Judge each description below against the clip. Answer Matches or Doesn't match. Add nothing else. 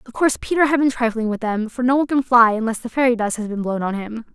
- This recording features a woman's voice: Matches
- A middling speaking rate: Doesn't match